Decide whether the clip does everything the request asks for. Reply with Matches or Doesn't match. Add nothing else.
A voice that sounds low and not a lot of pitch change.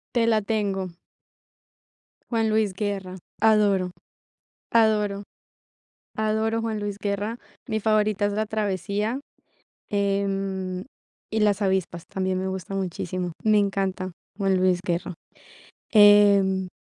Doesn't match